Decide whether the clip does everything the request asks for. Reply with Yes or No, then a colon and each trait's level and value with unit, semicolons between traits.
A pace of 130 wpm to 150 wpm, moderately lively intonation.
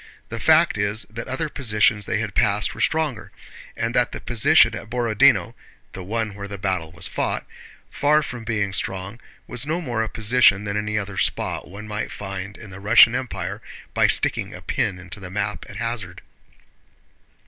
No: average, 180 wpm; average, 3.1 semitones